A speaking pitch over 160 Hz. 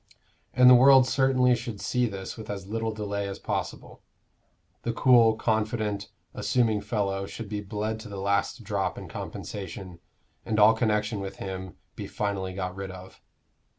No: low, 105 Hz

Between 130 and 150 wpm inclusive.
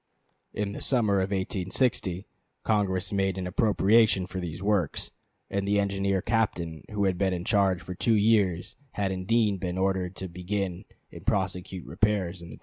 No: average, 175 wpm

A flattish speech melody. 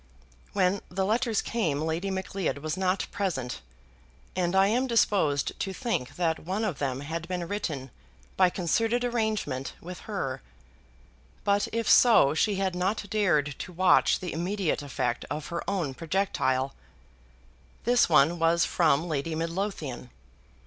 No: average, 4.8 semitones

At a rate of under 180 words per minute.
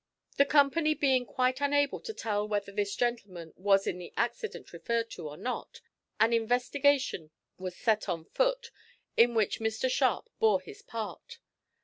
Yes: average, 155 wpm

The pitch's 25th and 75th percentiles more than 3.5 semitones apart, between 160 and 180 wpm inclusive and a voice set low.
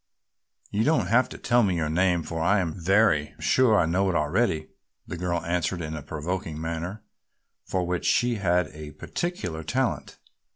Yes: average, 4.2 semitones; average, 175 wpm; very low, 90 Hz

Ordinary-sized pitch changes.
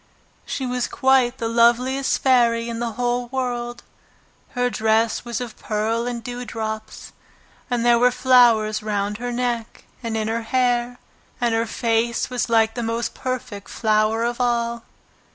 No: narrow, 1.6 semitones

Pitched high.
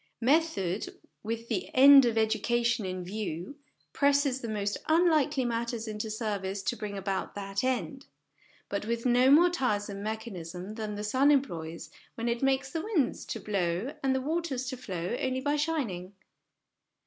Yes: high, 230 Hz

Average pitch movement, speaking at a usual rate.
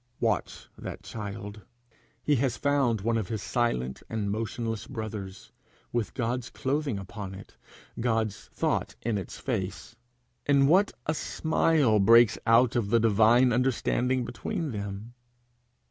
No: average, 3.4 semitones; slow, 130 wpm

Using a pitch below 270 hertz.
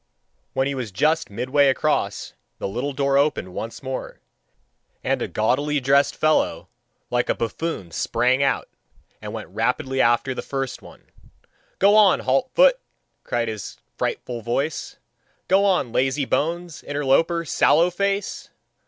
Yes: medium, 140 Hz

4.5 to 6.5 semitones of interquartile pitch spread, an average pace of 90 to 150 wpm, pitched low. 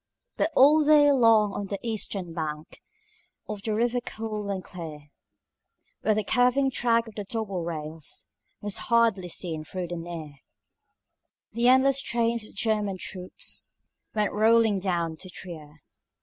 No: average, 5.0 semitones; average, 140 wpm; high, 205 Hz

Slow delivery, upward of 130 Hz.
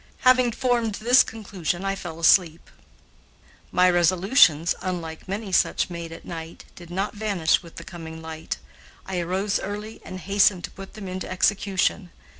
No: average, 155 wpm; medium, 185 Hz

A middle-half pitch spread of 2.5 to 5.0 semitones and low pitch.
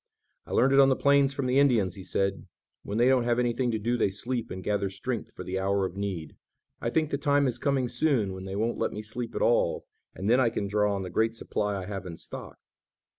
Yes: average, 4.6 semitones; low, 110 Hz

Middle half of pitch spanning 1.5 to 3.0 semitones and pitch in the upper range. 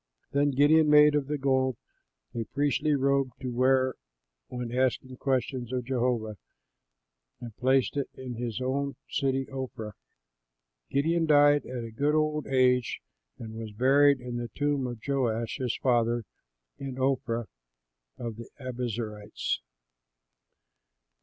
No: average, 2.7 semitones; low, 130 Hz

